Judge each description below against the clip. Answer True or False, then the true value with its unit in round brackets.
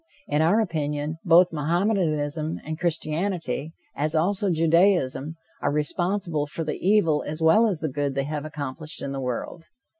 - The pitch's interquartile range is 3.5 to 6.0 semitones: False (2.9 semitones)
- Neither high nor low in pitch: True (155 Hz)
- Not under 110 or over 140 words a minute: False (155 wpm)